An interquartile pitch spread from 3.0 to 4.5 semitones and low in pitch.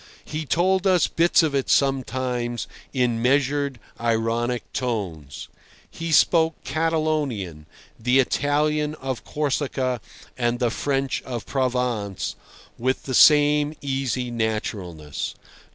Yes: average, 3.9 semitones; low, 130 Hz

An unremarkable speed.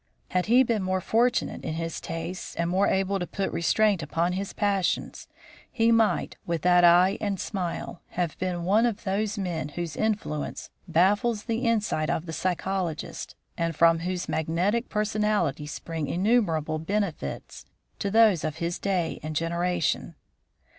Yes: average, 155 wpm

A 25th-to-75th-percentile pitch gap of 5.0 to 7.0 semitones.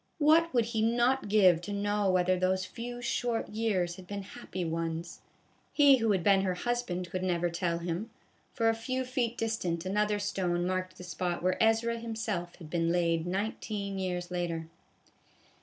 No: average, 4.2 semitones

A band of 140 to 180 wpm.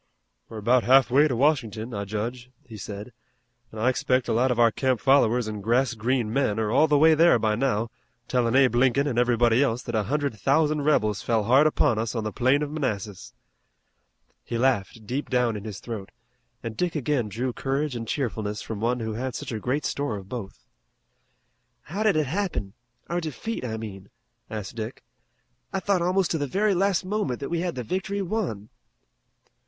No: average, 200 wpm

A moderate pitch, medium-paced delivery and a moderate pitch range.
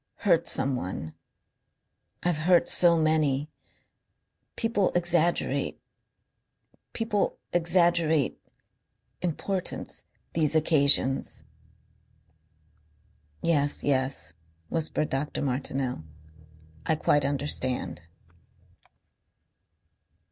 No: medium, 155 Hz; slow, 60 wpm; average, 4.0 semitones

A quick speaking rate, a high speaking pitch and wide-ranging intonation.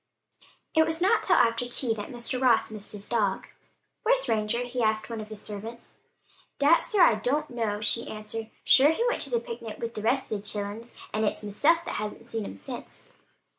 No: fast, 210 wpm; high, 230 Hz; average, 3.5 semitones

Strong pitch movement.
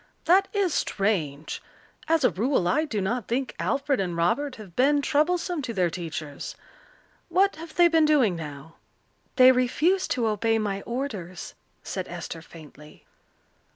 Yes: wide, 8.9 semitones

